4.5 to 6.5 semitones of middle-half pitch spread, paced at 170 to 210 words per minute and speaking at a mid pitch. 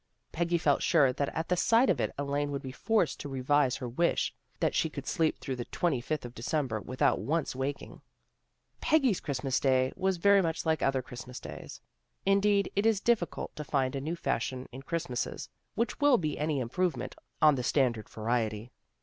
Yes: average, 5.0 semitones; average, 190 wpm; medium, 145 Hz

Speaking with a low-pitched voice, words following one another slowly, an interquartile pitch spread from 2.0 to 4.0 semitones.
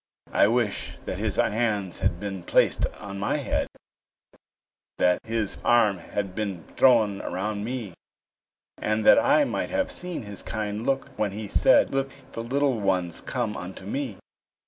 No: low, 105 Hz; average, 155 wpm; average, 3.7 semitones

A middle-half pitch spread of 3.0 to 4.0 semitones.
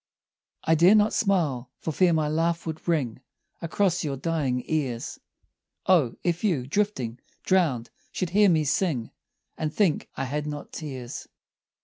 No: average, 4.9 semitones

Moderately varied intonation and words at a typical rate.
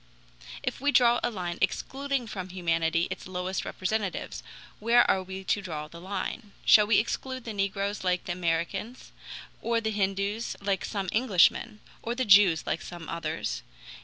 Yes: average, 3.9 semitones; average, 160 wpm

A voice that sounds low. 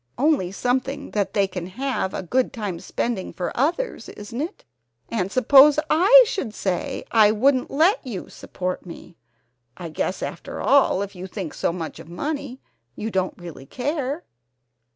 No: high, 225 Hz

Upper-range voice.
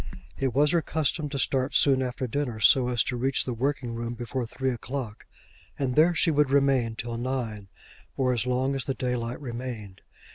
No: low, 130 Hz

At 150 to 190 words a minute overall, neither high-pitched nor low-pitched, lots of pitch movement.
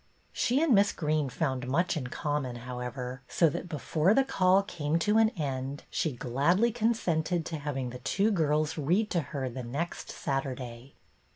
Yes: average, 175 wpm; medium, 150 Hz; wide, 5.7 semitones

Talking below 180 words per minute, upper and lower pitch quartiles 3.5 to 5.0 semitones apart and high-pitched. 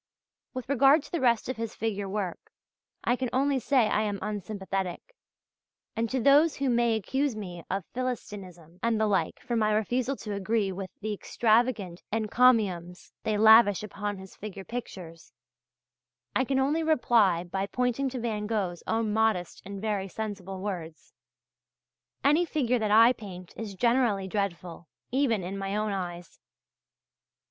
Yes: average, 155 wpm; average, 4.1 semitones; high, 215 Hz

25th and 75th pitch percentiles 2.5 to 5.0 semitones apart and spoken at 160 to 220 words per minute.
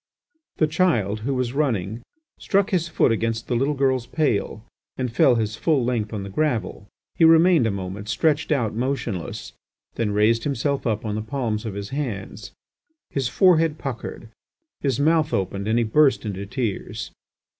No: wide, 5.4 semitones; average, 165 wpm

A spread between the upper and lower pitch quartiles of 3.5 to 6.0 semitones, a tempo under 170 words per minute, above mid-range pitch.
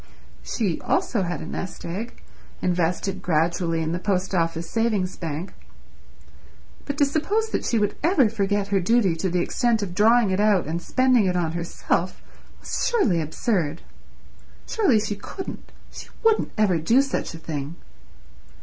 Yes: wide, 5.4 semitones; average, 160 wpm; high, 195 Hz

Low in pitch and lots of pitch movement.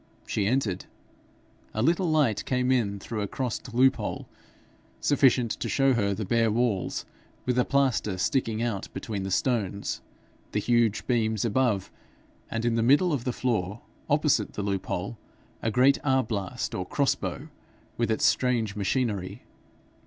No: low, 115 Hz; average, 4.0 semitones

